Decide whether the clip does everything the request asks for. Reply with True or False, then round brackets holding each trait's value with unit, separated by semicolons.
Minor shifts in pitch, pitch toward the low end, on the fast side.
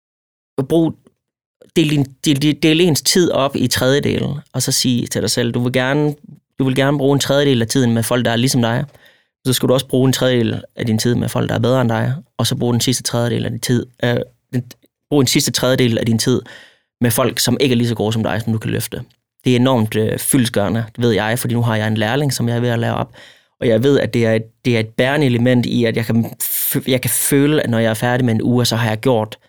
True (2.2 semitones; 125 Hz; 260 wpm)